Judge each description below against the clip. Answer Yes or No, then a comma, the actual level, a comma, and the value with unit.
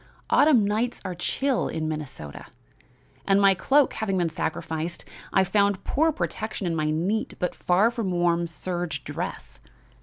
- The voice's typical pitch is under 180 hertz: No, medium, 185 Hz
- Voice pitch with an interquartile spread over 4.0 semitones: Yes, average, 4.4 semitones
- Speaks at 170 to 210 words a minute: No, average, 150 wpm